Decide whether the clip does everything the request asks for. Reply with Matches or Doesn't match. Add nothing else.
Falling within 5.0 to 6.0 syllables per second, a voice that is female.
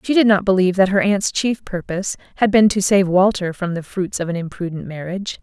Matches